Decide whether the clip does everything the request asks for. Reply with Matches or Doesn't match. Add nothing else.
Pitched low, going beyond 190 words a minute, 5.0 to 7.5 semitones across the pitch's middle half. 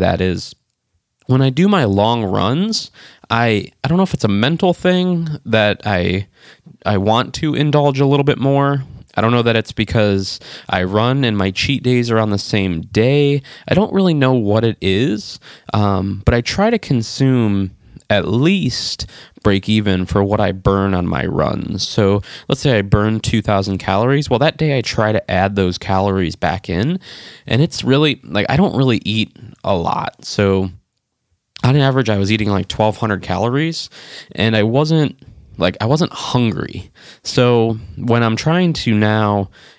Doesn't match